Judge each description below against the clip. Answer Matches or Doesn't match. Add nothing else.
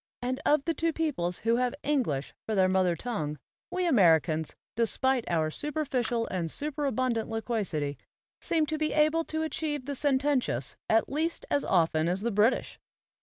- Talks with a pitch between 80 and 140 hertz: Doesn't match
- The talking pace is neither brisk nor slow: Matches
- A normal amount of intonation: Doesn't match